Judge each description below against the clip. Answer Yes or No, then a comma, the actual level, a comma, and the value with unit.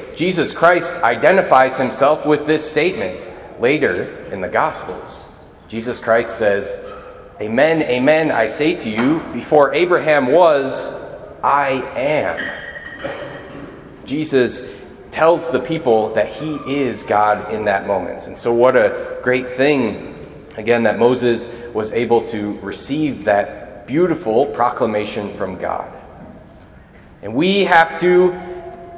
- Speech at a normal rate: No, slow, 120 wpm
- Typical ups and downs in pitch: No, wide, 6.0 semitones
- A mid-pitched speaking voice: No, low, 130 Hz